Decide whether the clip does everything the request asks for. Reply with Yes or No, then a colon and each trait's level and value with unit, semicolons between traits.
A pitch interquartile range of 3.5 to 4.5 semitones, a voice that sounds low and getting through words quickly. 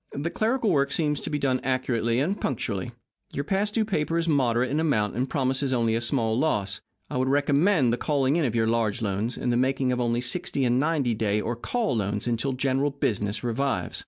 Yes: average, 3.8 semitones; low, 130 Hz; fast, 215 wpm